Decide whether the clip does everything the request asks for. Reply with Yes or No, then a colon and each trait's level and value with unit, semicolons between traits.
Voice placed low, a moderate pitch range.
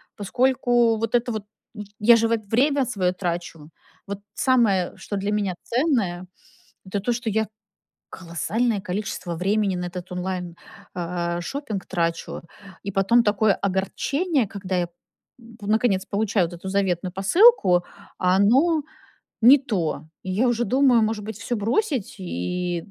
No: high, 200 Hz; average, 4.5 semitones